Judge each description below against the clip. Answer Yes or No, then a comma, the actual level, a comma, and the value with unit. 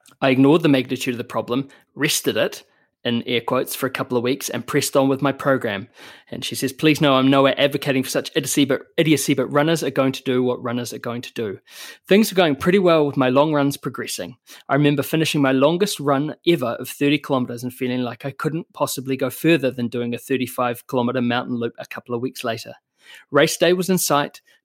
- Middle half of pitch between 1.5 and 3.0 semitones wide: Yes, average, 2.7 semitones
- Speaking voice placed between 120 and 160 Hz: Yes, low, 135 Hz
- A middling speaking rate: No, fast, 225 wpm